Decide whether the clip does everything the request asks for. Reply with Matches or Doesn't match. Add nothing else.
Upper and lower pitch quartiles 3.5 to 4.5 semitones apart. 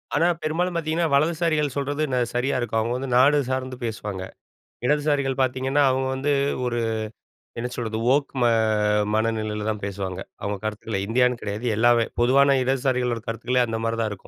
Matches